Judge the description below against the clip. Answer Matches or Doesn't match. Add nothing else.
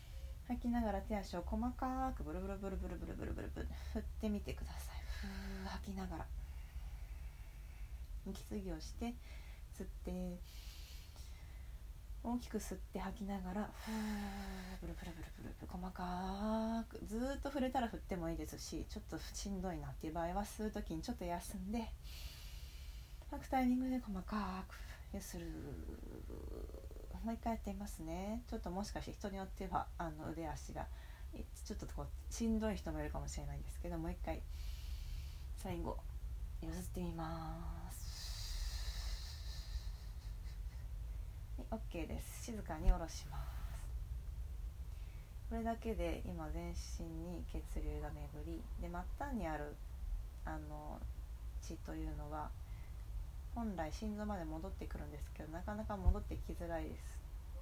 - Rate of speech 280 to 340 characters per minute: Matches